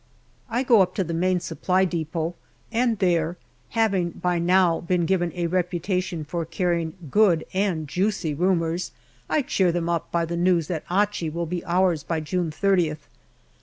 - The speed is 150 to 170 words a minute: Yes, average, 165 wpm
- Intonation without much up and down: Yes, narrow, 2.1 semitones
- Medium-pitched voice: Yes, medium, 175 Hz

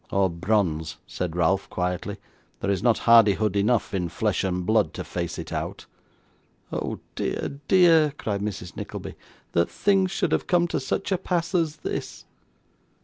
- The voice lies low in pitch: Yes, low, 105 Hz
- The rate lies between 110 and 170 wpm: Yes, average, 160 wpm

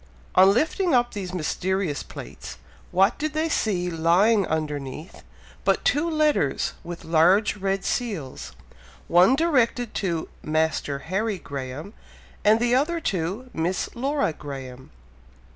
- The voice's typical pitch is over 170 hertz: Yes, high, 190 Hz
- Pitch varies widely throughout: Yes, wide, 7.1 semitones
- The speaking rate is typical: No, slow, 125 wpm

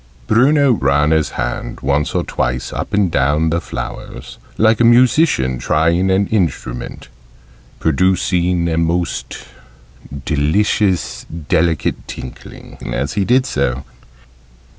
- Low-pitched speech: Yes, very low, 85 Hz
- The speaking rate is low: Yes, slow, 115 wpm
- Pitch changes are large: Yes, wide, 6.3 semitones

